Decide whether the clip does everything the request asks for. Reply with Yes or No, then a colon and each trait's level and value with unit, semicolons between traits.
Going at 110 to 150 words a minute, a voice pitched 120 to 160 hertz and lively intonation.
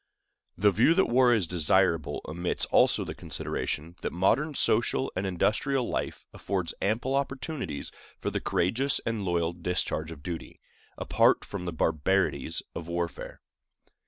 No: average, 140 wpm; very low, 95 Hz; wide, 5.9 semitones